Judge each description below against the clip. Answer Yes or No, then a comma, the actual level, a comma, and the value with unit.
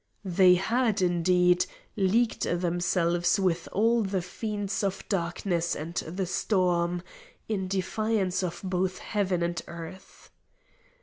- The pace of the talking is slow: Yes, slow, 115 wpm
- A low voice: No, medium, 185 Hz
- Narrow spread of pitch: Yes, narrow, 2.2 semitones